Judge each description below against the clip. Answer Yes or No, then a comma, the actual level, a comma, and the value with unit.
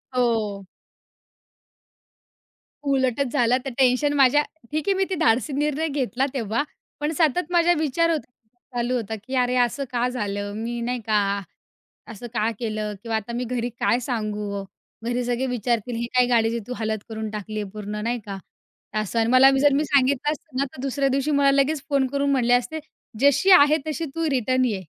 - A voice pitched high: Yes, very high, 250 Hz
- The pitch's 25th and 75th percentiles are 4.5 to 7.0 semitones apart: No, average, 3.6 semitones